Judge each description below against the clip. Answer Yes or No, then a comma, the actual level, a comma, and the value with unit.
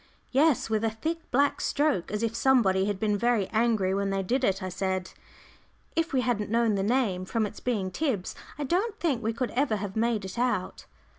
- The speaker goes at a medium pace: No, fast, 210 wpm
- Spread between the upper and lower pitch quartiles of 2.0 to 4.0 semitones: No, average, 4.7 semitones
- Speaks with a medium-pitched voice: No, high, 225 Hz